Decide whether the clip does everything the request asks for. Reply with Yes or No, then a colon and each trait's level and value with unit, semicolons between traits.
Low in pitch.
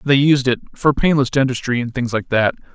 Yes: low, 130 Hz